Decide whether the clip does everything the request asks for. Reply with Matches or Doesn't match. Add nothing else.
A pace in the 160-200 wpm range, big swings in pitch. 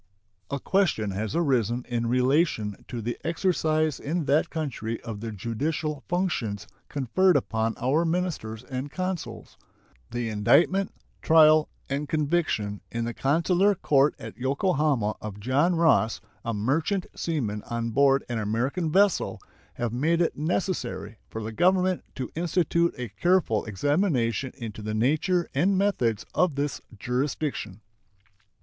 Doesn't match